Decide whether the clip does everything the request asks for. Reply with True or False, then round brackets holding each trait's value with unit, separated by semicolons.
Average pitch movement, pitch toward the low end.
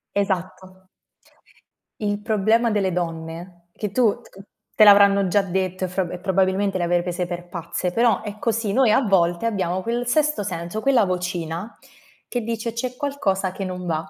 False (3.5 semitones; 195 Hz)